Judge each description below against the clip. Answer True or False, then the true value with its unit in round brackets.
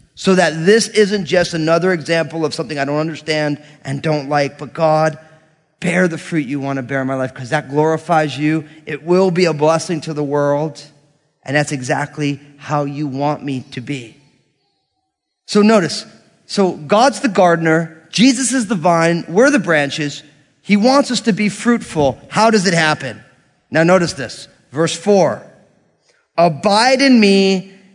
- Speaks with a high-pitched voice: False (160 Hz)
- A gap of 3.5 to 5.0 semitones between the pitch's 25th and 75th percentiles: True (4.4 semitones)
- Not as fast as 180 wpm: True (170 wpm)